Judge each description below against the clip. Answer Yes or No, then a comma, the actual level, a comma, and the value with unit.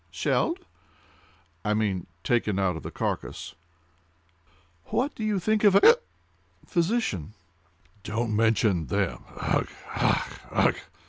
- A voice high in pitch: No, low, 115 Hz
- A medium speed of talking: No, slow, 110 wpm